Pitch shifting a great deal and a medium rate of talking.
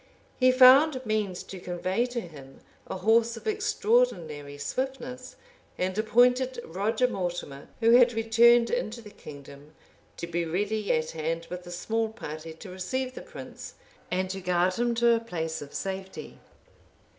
Yes: wide, 5.7 semitones; average, 155 wpm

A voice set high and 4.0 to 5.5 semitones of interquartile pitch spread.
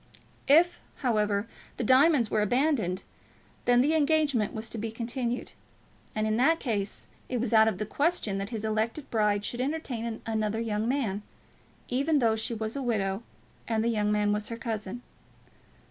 No: high, 225 Hz; average, 3.3 semitones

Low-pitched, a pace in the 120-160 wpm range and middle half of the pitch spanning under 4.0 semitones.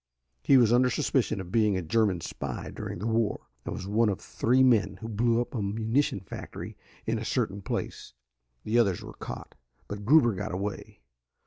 No: low, 110 Hz; average, 190 wpm; average, 3.1 semitones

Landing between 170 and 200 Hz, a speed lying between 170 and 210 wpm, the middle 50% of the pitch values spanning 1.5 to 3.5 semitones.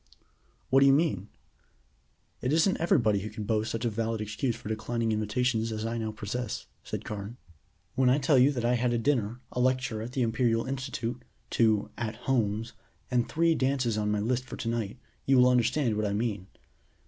No: low, 115 Hz; average, 195 wpm; average, 2.9 semitones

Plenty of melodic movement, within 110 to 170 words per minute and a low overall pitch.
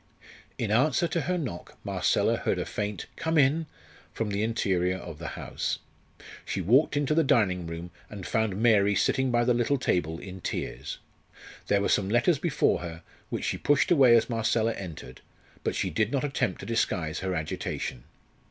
No: wide, 6.2 semitones; average, 180 wpm; low, 110 Hz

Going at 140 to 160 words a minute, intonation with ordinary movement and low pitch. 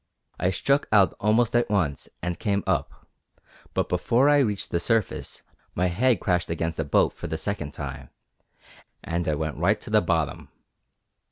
No: average, 170 wpm; average, 5.0 semitones; very low, 90 Hz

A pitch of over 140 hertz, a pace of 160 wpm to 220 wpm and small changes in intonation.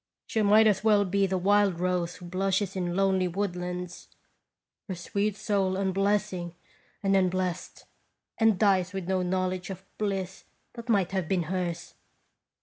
No: high, 190 Hz; average, 145 wpm; narrow, 1.9 semitones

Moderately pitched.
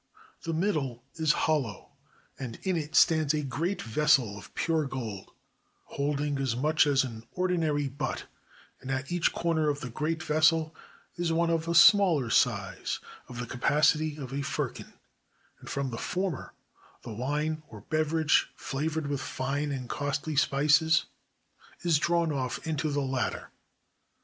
Yes: medium, 150 Hz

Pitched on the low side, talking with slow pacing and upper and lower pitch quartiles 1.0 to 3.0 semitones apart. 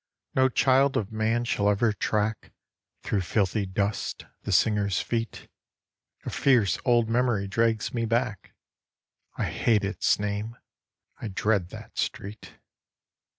Yes: low, 110 Hz; slow, 125 wpm; narrow, 2.4 semitones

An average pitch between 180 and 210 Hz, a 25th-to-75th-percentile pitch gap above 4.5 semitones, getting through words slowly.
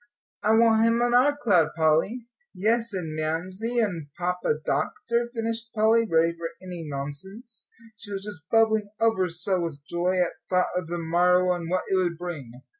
No: medium, 185 Hz; average, 5.1 semitones; average, 175 wpm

